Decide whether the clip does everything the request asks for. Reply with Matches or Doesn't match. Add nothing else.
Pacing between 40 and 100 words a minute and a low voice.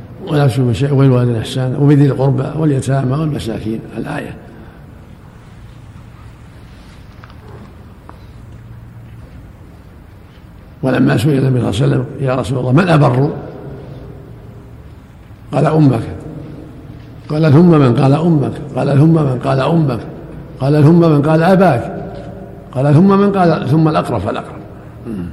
Doesn't match